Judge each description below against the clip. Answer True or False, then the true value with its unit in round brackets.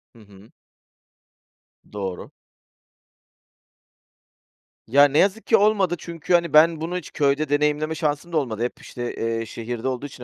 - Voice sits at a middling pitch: True (145 Hz)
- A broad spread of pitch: True (5.8 semitones)